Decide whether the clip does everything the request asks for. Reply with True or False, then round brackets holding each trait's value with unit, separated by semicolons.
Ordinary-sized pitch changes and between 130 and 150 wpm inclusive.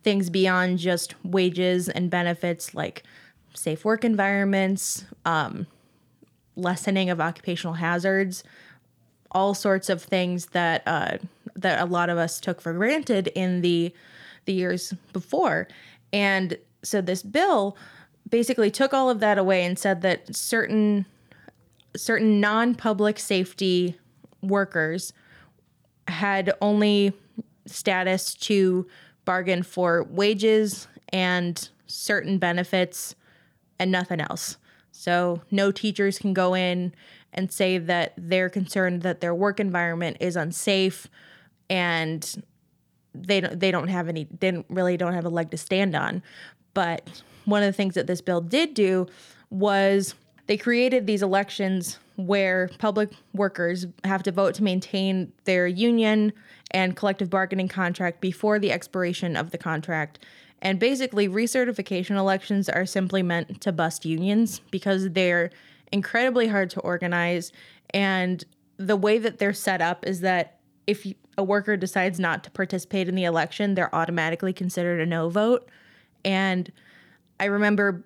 False (2.2 semitones; 135 wpm)